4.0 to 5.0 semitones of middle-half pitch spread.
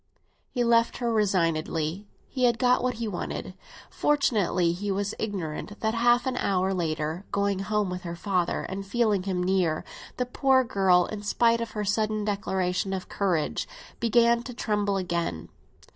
Yes: average, 4.3 semitones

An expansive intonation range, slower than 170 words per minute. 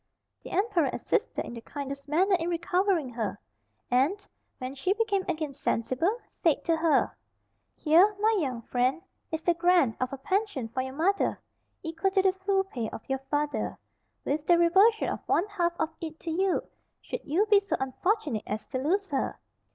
No: wide, 6.1 semitones; average, 175 wpm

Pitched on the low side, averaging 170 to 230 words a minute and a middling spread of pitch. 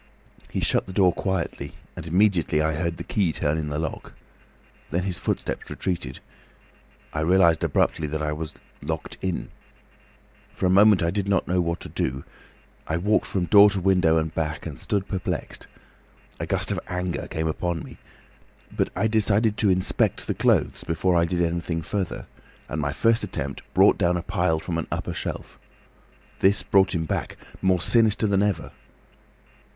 Yes: very low, 90 Hz; average, 175 wpm; average, 3.2 semitones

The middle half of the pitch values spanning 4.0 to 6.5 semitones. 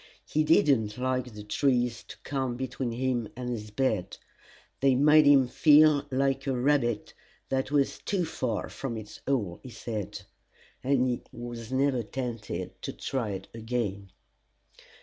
No: average, 3.2 semitones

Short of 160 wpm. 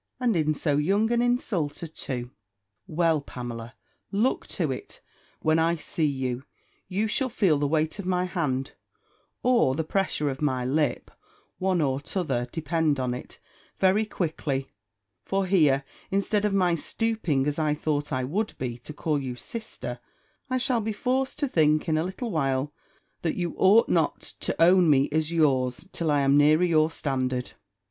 No: average, 170 wpm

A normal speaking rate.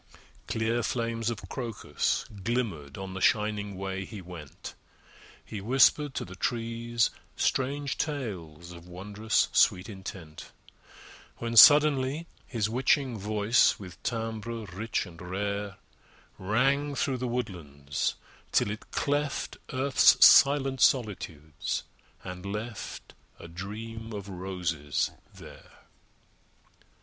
No: slow, 110 wpm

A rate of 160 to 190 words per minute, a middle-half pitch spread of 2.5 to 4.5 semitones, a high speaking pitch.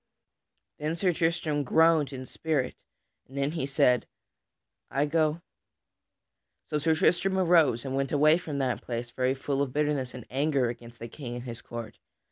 No: average, 165 wpm; average, 3.8 semitones; medium, 140 Hz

